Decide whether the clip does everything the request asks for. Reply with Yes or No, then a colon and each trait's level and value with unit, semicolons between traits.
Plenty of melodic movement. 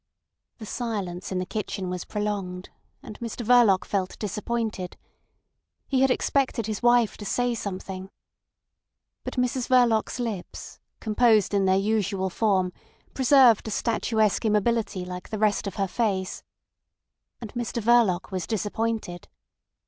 No: average, 3.7 semitones